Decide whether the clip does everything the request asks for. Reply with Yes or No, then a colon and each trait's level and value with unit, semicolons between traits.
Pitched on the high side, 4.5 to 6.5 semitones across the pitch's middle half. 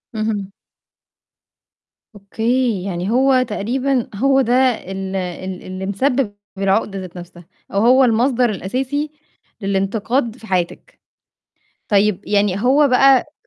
Yes: high, 215 Hz; average, 4.8 semitones